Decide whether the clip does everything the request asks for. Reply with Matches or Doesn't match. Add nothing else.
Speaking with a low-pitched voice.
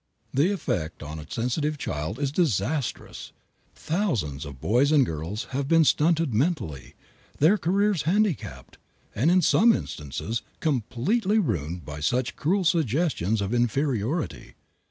Matches